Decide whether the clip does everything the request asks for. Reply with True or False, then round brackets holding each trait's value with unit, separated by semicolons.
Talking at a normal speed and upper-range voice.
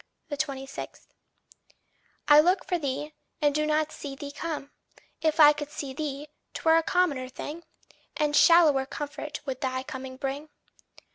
True (145 wpm; 295 Hz)